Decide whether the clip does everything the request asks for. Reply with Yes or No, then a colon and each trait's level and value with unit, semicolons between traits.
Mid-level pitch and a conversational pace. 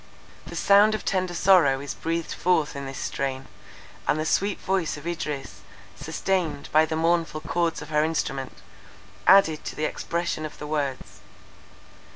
Yes: medium, 160 Hz; average, 160 wpm